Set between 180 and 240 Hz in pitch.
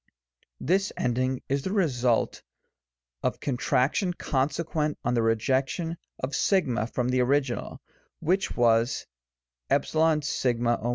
No: low, 130 Hz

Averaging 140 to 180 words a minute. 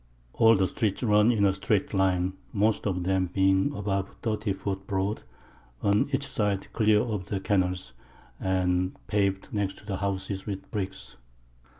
Yes: average, 155 wpm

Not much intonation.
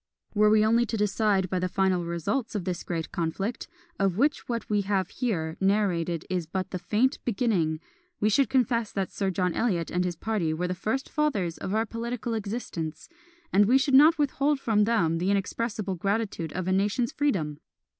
No: average, 4.4 semitones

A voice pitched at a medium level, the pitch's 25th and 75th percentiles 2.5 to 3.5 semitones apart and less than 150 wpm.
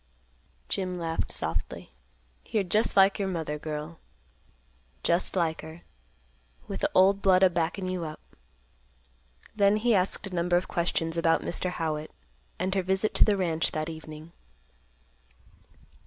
Yes: medium, 175 Hz; average, 2.9 semitones; average, 140 wpm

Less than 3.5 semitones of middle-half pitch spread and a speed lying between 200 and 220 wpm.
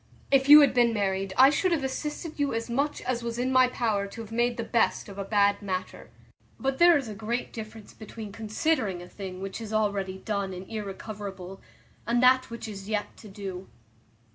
No: average, 4.1 semitones; fast, 205 wpm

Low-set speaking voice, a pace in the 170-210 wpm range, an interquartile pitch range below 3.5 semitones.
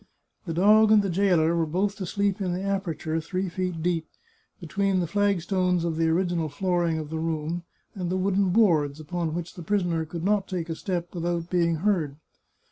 No: medium, 175 Hz; average, 200 wpm; average, 2.8 semitones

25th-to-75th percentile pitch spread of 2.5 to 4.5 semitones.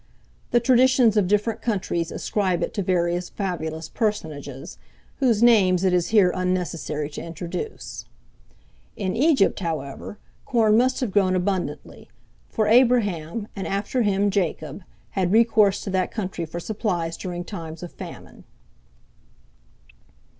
Yes: average, 4.0 semitones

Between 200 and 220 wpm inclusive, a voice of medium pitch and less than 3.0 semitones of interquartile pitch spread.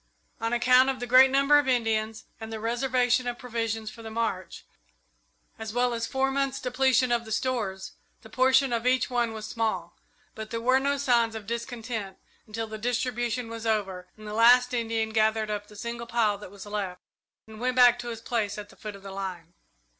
No: fast, 205 wpm; high, 230 Hz; narrow, 2.4 semitones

